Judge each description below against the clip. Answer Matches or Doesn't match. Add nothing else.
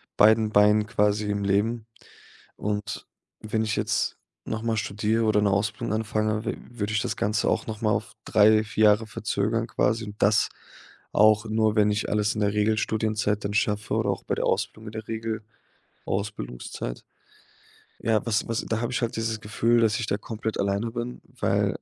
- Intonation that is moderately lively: Doesn't match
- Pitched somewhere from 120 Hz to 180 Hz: Doesn't match